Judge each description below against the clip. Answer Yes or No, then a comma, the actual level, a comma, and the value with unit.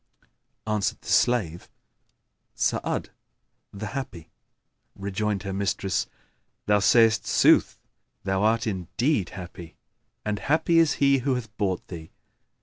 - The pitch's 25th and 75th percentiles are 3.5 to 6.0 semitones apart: Yes, average, 3.9 semitones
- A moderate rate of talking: No, slow, 115 wpm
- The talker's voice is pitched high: No, low, 105 Hz